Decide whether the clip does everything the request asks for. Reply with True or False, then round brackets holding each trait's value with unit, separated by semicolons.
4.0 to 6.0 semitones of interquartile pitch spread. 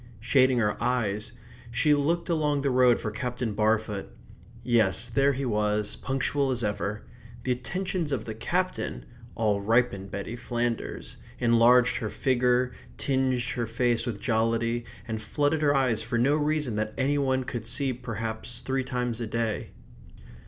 False (3.1 semitones)